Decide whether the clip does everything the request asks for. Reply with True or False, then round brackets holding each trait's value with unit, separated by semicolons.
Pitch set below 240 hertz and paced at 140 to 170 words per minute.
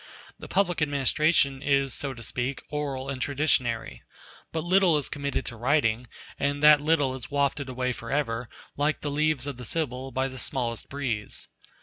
True (140 Hz; 165 wpm)